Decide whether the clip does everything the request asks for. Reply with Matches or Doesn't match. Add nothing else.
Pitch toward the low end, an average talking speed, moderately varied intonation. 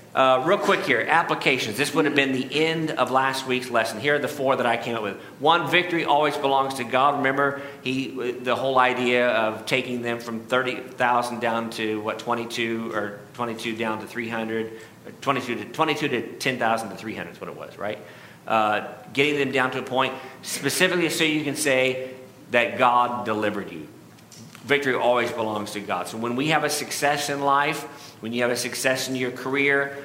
Matches